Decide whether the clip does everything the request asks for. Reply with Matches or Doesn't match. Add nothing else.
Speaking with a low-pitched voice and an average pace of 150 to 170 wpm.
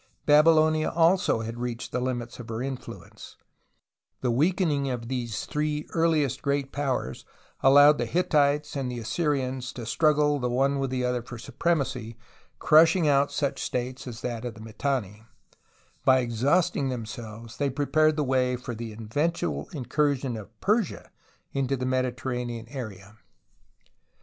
Matches